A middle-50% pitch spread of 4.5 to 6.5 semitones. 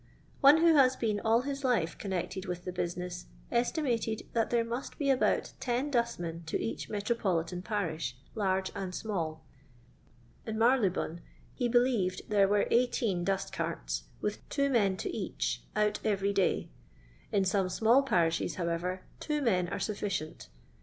Yes: average, 4.8 semitones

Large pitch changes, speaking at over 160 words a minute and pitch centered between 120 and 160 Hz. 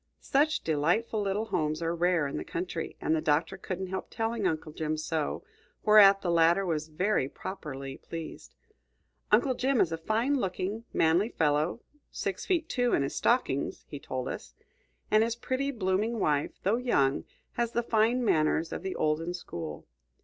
No: wide, 6.2 semitones; average, 170 wpm; medium, 185 Hz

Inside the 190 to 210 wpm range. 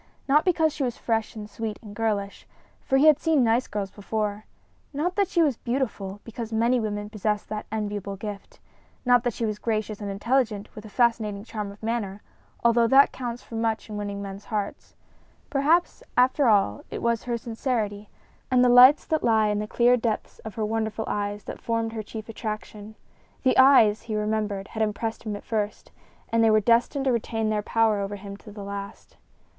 Yes: average, 195 wpm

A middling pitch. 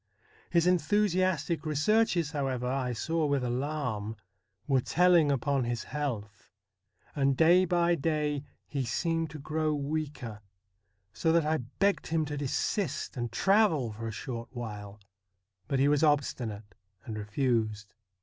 Yes: medium, 145 Hz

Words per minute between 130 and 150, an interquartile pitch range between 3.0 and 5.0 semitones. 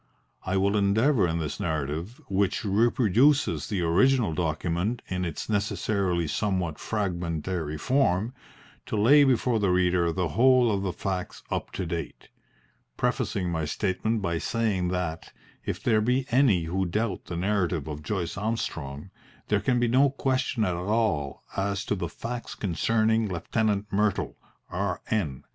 Yes: average, 145 wpm; average, 4.4 semitones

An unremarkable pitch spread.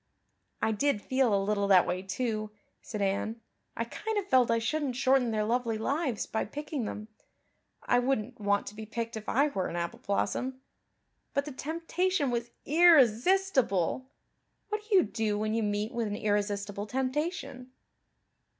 Yes: average, 4.8 semitones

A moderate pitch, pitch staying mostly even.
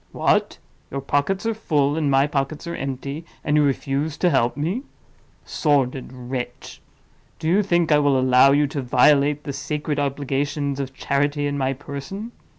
Yes: medium, 145 Hz; narrow, 1.8 semitones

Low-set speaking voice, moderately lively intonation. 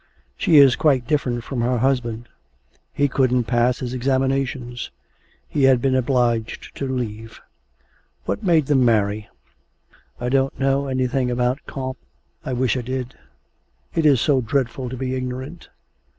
No: low, 130 Hz; narrow, 1.9 semitones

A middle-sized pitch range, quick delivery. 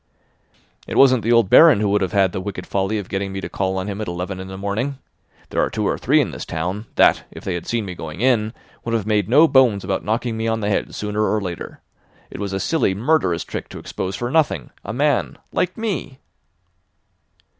Yes: average, 3.8 semitones; fast, 230 wpm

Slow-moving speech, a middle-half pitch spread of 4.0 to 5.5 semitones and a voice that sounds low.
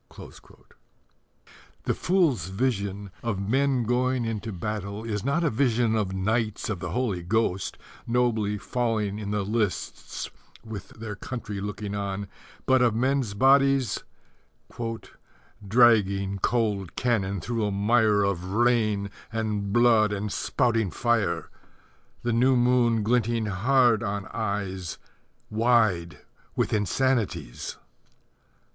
No: slow, 115 wpm; average, 3.2 semitones; low, 110 Hz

